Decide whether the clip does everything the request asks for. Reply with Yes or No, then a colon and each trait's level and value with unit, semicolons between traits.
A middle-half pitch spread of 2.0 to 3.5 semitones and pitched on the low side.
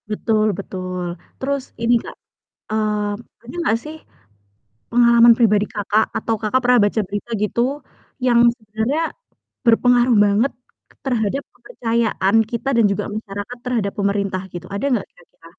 No: average, 2.8 semitones; high, 220 Hz